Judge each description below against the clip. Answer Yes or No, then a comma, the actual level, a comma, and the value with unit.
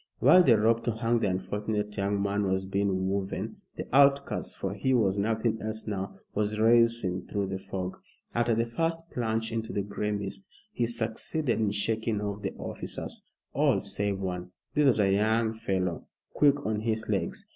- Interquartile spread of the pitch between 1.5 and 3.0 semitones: Yes, average, 2.7 semitones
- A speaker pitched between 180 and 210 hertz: No, low, 105 Hz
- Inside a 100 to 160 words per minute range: No, average, 180 wpm